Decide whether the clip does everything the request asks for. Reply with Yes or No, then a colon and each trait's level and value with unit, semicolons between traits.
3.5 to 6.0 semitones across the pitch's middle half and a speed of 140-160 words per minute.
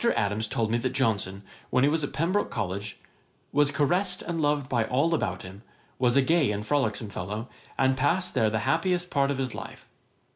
No: average, 5.2 semitones; average, 195 wpm